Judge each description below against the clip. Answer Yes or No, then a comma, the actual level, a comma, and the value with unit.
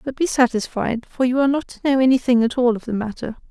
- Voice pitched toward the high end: Yes, very high, 250 Hz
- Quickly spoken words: Yes, fast, 255 wpm